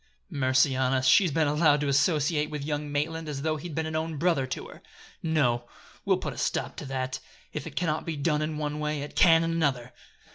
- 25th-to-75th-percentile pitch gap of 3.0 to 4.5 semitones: No, narrow, 2.5 semitones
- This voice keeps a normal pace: No, fast, 230 wpm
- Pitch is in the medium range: Yes, medium, 150 Hz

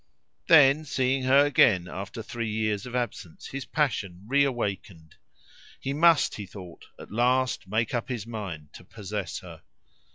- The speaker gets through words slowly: No, average, 150 wpm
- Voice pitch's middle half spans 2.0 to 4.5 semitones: No, average, 5.0 semitones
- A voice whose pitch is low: Yes, low, 115 Hz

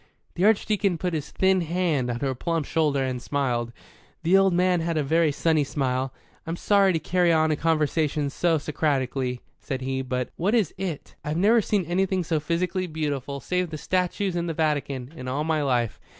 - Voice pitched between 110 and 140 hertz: No, medium, 160 Hz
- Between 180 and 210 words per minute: Yes, average, 195 wpm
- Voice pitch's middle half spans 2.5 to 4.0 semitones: No, average, 4.5 semitones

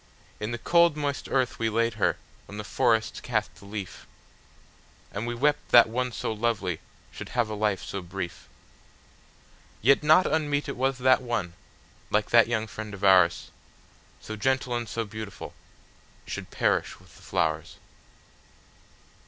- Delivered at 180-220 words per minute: No, average, 145 wpm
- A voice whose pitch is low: Yes, low, 115 Hz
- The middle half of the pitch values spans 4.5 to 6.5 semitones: No, average, 3.7 semitones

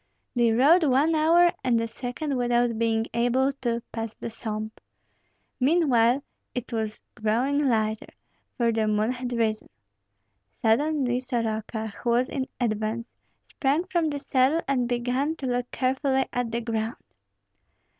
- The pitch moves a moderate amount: Yes, average, 3.0 semitones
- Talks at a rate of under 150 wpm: Yes, average, 140 wpm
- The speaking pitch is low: No, high, 245 Hz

